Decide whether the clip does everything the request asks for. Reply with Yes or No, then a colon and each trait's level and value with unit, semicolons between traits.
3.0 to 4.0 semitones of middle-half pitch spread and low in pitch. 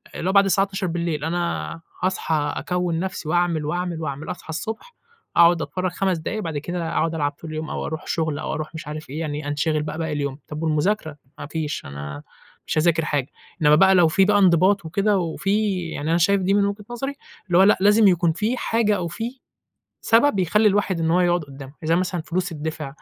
No: average, 3.7 semitones; medium, 170 Hz